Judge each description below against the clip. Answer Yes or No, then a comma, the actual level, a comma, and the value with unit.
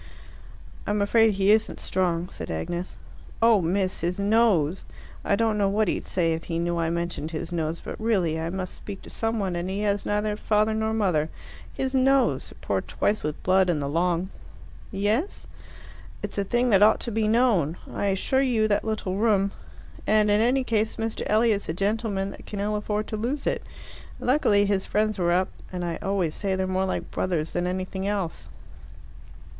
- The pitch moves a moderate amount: Yes, average, 3.4 semitones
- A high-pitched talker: Yes, high, 200 Hz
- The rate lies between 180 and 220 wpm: Yes, average, 190 wpm